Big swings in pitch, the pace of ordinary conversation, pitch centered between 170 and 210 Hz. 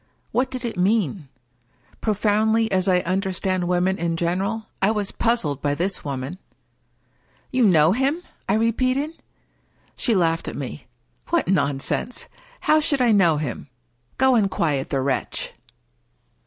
Yes: wide, 5.7 semitones; average, 155 wpm; high, 190 Hz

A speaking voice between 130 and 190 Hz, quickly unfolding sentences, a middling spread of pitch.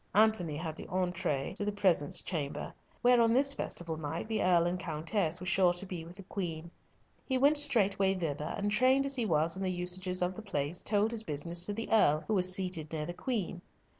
Yes: medium, 185 Hz; fast, 220 wpm; average, 4.2 semitones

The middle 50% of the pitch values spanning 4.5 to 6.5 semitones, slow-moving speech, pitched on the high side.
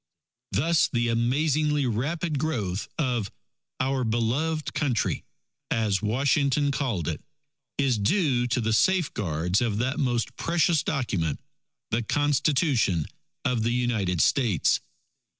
No: average, 4.9 semitones; slow, 115 wpm; low, 125 Hz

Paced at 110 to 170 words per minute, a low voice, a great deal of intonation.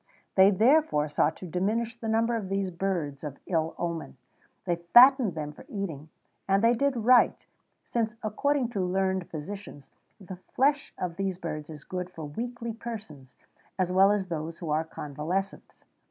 No: average, 165 wpm; high, 190 Hz; wide, 5.7 semitones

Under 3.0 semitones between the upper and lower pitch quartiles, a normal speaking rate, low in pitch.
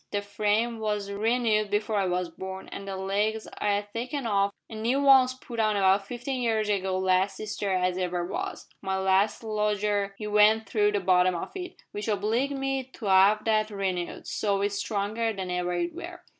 No: narrow, 2.5 semitones; average, 195 wpm; high, 210 Hz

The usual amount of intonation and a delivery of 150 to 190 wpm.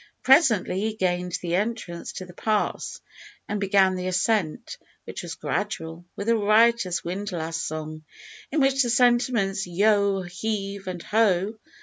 No: average, 3.8 semitones; average, 140 wpm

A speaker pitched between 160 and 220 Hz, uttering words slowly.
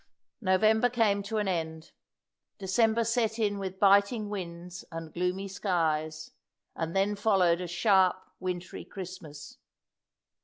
Yes: high, 190 Hz; slow, 125 wpm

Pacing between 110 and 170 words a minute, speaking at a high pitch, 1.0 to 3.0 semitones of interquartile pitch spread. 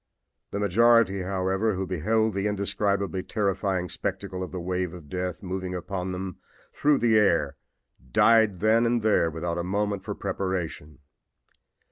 No: average, 145 wpm; very low, 95 Hz; narrow, 2.4 semitones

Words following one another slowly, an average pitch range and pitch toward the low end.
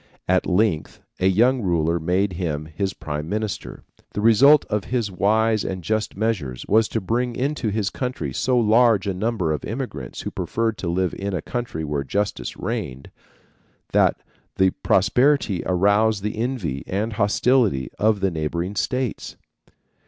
No: average, 155 wpm; average, 4.2 semitones; low, 100 Hz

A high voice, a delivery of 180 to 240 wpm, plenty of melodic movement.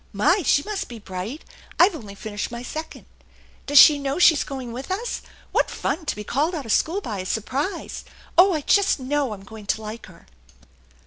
Yes: very high, 275 Hz; average, 200 wpm; wide, 6.7 semitones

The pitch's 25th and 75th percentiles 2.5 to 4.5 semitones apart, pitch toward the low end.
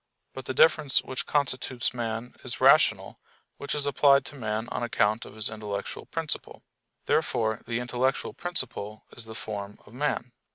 Yes: average, 3.5 semitones; low, 120 Hz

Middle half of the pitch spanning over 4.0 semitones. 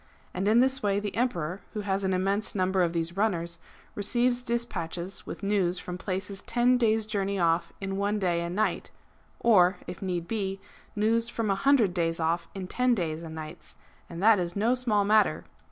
No: average, 3.6 semitones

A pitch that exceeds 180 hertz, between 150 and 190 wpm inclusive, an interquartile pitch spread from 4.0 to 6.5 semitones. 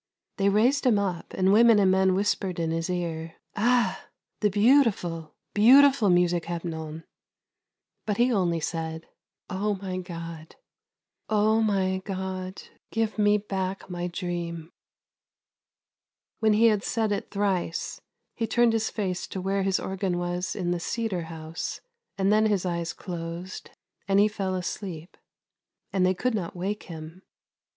No: high, 190 Hz; average, 155 wpm; average, 3.2 semitones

